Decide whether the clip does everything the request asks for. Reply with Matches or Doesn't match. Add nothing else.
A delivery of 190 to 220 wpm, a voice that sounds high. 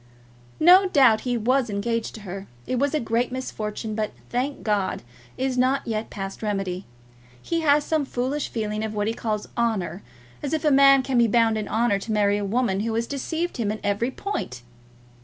Matches